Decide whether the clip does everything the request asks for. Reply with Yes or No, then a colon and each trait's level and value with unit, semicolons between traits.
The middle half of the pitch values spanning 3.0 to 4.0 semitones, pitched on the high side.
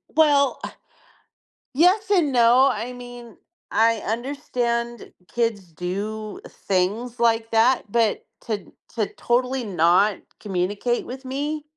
Yes: average, 3.4 semitones; high, 235 Hz